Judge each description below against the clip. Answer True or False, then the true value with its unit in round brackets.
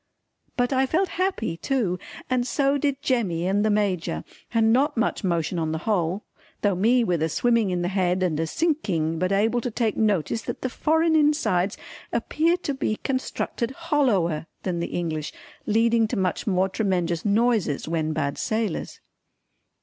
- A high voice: True (210 Hz)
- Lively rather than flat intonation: True (6.3 semitones)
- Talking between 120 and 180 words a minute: True (170 wpm)